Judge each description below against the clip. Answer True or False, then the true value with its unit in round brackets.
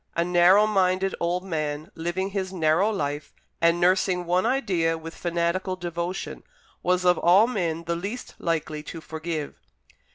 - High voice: False (175 Hz)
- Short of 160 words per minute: True (150 wpm)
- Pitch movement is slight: True (2.3 semitones)